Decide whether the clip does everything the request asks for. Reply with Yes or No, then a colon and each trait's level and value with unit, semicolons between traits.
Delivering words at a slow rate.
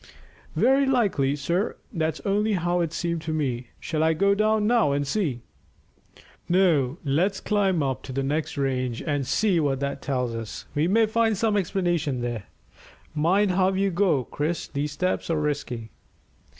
No: average, 165 wpm